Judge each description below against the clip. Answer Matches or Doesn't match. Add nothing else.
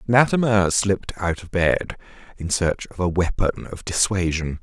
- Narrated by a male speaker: Matches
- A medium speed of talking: Matches